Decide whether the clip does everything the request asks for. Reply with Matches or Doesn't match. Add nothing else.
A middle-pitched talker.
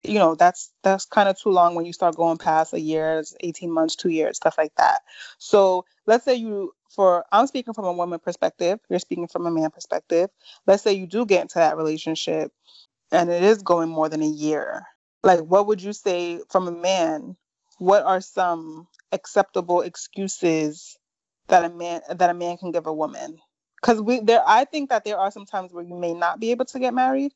Matches